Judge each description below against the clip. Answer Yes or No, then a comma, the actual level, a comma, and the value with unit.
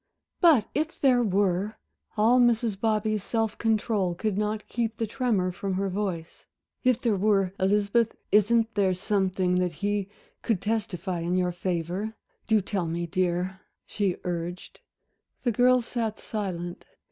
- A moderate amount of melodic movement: Yes, average, 3.4 semitones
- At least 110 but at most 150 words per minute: Yes, average, 145 wpm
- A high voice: Yes, high, 205 Hz